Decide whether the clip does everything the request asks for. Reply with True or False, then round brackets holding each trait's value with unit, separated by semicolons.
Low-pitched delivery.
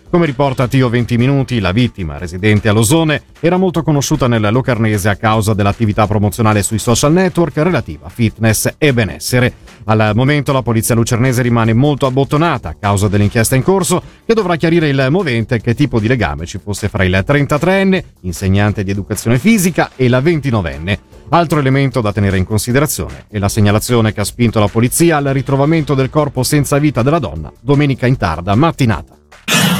True (120 Hz)